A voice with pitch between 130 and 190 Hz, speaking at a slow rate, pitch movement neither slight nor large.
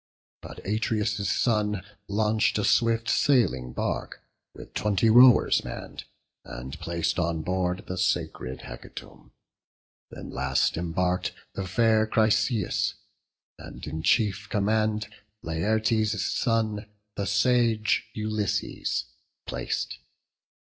No: low, 105 Hz; slow, 100 wpm; average, 3.5 semitones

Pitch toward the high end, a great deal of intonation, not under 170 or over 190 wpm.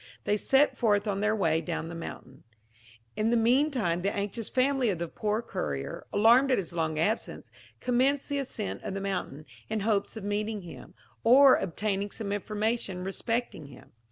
No: high, 210 Hz; average, 4.3 semitones; average, 180 wpm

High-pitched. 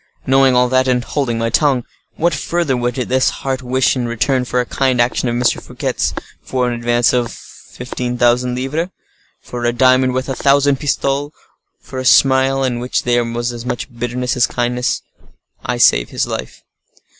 No: low, 125 Hz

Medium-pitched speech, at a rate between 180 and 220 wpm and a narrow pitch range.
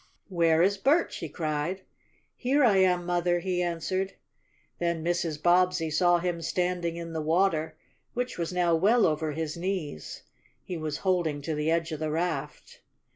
No: medium, 170 Hz; average, 165 wpm; narrow, 2.3 semitones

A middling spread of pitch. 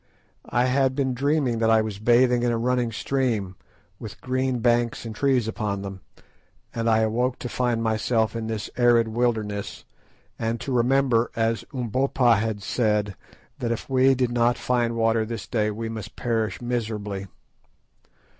No: narrow, 2.1 semitones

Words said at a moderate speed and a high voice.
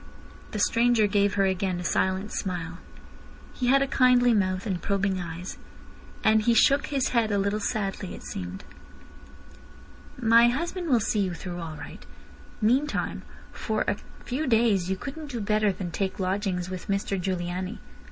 Yes: average, 160 wpm; high, 200 Hz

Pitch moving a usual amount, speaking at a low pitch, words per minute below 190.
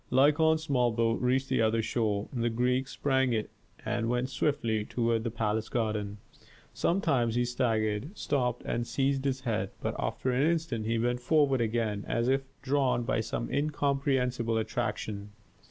Yes: average, 3.1 semitones; low, 120 Hz; average, 160 wpm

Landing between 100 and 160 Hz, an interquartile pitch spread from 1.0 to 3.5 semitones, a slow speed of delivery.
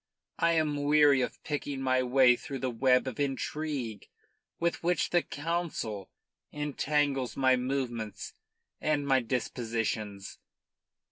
Yes: low, 135 Hz; average, 3.1 semitones; slow, 120 wpm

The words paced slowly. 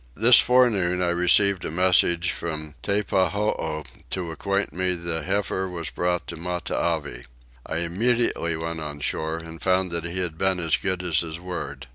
No: average, 165 wpm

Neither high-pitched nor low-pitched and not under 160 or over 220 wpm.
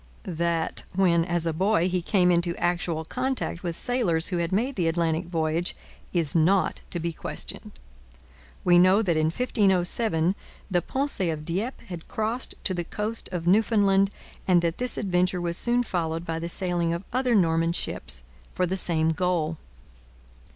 Yes: medium, 175 Hz; average, 165 wpm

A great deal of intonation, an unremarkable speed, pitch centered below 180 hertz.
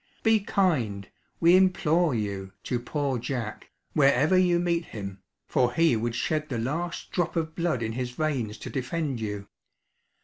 Yes: wide, 6.6 semitones; average, 160 wpm; medium, 140 Hz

